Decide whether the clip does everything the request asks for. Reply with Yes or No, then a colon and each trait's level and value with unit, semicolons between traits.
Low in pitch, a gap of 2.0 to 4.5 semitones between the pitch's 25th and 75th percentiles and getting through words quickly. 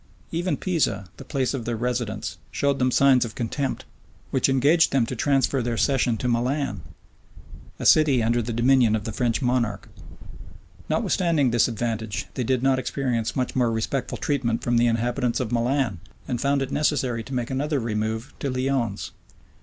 No: low, 125 Hz; average, 2.9 semitones; average, 170 wpm